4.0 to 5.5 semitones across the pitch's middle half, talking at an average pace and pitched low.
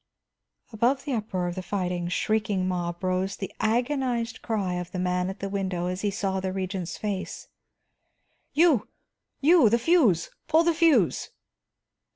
No: average, 4.5 semitones; average, 155 wpm; high, 195 Hz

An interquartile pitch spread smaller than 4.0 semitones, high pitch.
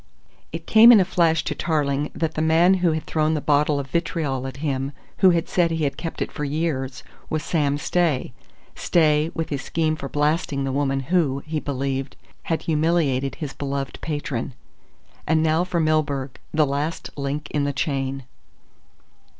No: average, 2.8 semitones; medium, 150 Hz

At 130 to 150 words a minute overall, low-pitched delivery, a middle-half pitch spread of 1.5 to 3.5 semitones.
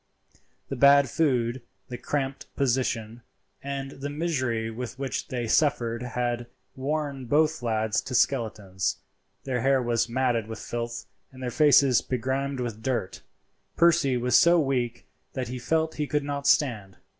Yes: average, 140 wpm; low, 130 Hz; average, 3.0 semitones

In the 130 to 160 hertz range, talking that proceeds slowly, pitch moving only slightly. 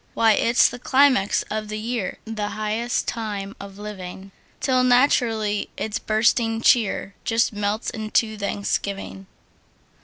No: high, 215 Hz; slow, 125 wpm; narrow, 2.2 semitones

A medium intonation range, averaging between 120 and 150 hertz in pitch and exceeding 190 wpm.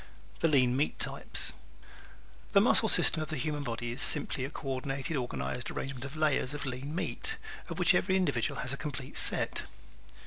No: average, 3.3 semitones; medium, 140 Hz; average, 185 wpm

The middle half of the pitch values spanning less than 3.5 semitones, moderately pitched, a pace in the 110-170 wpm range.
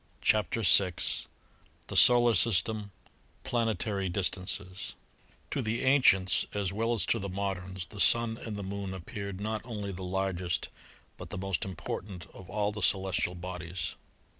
No: average, 2.8 semitones; low, 100 Hz; average, 150 wpm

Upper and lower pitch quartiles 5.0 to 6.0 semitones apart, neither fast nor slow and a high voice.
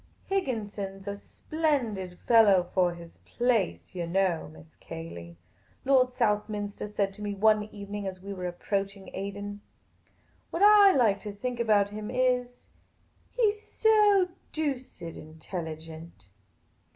No: average, 5.3 semitones; slow, 130 wpm; high, 205 Hz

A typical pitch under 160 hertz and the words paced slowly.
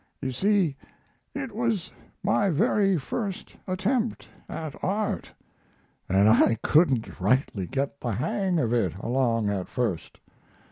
Yes: medium, 140 Hz; slow, 125 wpm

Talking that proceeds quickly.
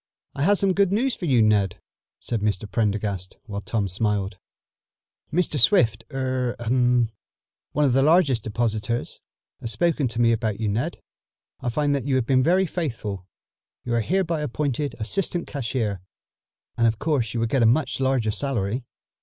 No: average, 170 wpm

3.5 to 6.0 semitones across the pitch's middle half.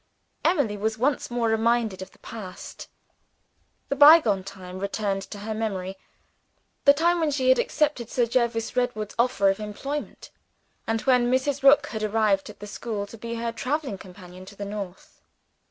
Yes: average, 4.2 semitones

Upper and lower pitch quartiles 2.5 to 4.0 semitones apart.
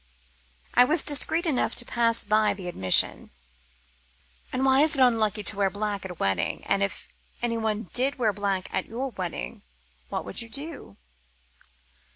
No: average, 4.6 semitones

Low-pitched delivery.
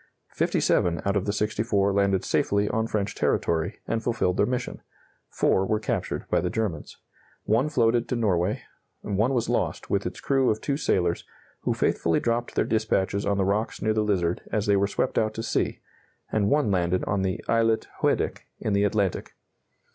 Yes: low, 105 Hz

